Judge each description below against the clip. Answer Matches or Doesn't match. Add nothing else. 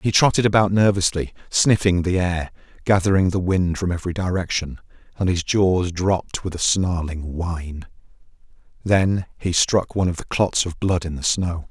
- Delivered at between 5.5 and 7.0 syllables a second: Doesn't match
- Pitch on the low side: Matches